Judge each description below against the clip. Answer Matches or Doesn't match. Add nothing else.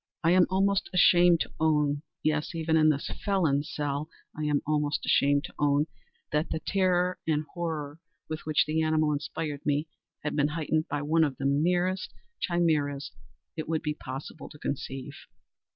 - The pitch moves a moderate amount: Doesn't match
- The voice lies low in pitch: Doesn't match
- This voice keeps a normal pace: Matches